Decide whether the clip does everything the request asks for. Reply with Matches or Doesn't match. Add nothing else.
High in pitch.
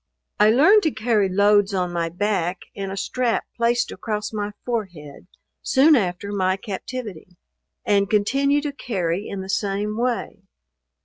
Matches